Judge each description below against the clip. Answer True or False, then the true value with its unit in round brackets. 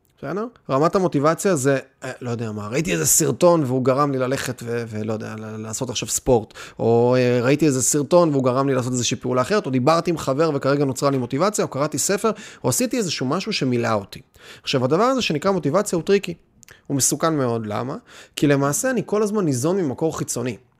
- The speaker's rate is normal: False (190 wpm)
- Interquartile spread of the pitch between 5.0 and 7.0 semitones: True (5.5 semitones)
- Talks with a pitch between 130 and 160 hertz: True (140 Hz)